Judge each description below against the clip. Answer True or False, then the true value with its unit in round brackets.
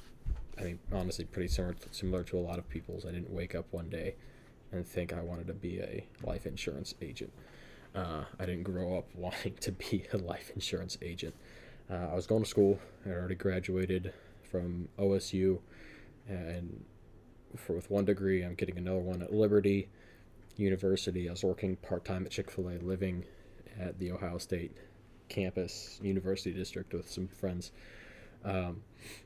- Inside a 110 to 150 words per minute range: False (165 wpm)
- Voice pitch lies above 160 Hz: False (95 Hz)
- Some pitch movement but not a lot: False (2.1 semitones)